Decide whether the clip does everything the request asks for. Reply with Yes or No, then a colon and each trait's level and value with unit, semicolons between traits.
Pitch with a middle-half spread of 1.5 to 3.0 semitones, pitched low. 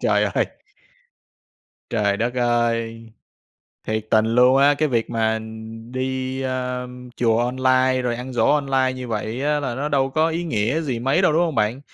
Yes: narrow, 2.6 semitones; low, 130 Hz